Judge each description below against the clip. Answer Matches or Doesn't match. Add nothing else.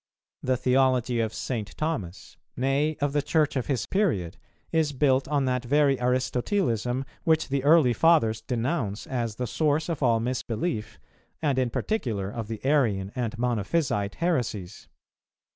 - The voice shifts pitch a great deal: Doesn't match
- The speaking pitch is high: Doesn't match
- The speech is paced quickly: Doesn't match